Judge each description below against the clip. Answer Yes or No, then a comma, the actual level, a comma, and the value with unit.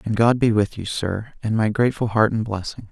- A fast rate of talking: Yes, fast, 245 wpm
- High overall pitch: No, low, 110 Hz